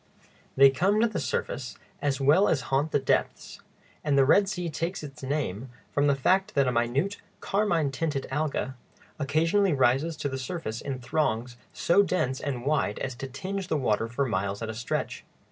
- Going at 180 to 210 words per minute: Yes, average, 185 wpm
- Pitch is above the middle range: No, medium, 140 Hz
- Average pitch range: Yes, average, 4.2 semitones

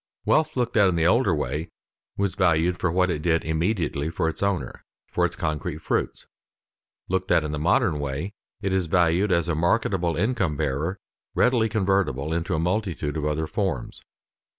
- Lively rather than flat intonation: No, average, 3.7 semitones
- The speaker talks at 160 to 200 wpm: Yes, average, 175 wpm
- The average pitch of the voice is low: Yes, very low, 85 Hz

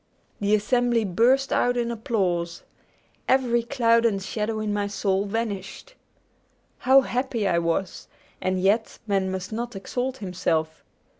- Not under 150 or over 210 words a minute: No, slow, 135 wpm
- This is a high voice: Yes, high, 215 Hz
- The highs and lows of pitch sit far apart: No, average, 3.8 semitones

